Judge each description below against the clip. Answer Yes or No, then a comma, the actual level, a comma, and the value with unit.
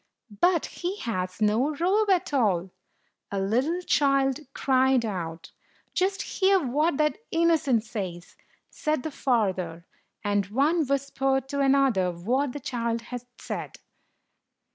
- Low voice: No, very high, 265 Hz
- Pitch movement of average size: No, wide, 6.5 semitones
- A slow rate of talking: Yes, slow, 125 wpm